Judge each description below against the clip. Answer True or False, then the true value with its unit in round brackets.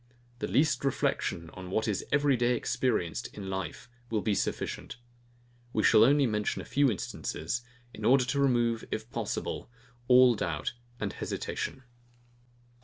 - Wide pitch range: False (4.4 semitones)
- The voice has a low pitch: True (120 Hz)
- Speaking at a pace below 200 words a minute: True (145 wpm)